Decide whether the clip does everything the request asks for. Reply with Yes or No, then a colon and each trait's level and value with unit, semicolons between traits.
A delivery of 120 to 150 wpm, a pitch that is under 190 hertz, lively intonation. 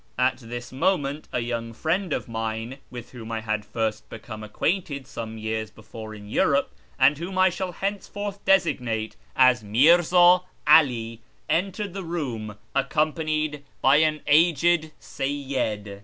Yes: average, 140 wpm; low, 135 Hz; wide, 6.9 semitones